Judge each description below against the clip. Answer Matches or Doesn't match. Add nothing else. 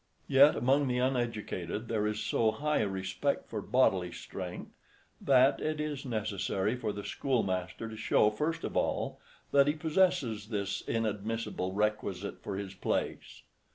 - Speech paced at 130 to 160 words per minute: Matches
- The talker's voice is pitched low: Matches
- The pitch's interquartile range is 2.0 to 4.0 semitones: Doesn't match